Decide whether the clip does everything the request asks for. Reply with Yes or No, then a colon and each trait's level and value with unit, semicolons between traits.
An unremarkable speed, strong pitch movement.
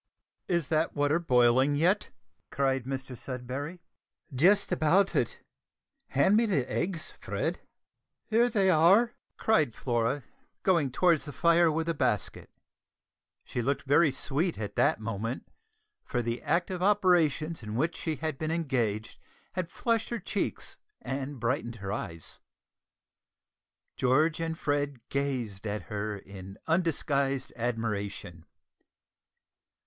No: slow, 125 wpm; wide, 5.9 semitones